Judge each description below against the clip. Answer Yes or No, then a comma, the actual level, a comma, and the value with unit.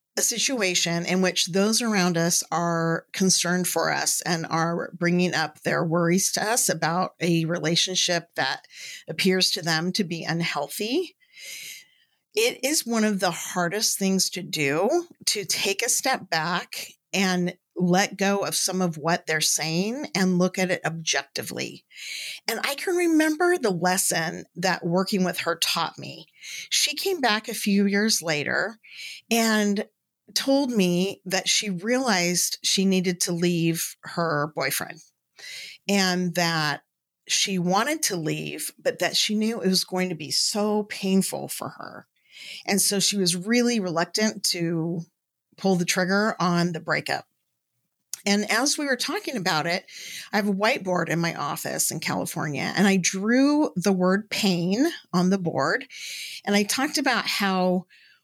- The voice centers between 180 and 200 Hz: Yes, medium, 185 Hz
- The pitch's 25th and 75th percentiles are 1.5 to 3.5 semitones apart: No, average, 3.9 semitones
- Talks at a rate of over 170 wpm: No, average, 155 wpm